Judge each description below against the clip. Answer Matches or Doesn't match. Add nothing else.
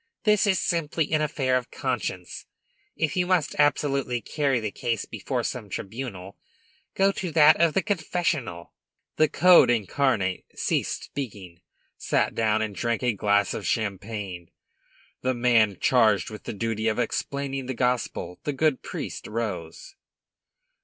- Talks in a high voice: Doesn't match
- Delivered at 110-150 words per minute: Matches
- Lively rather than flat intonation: Matches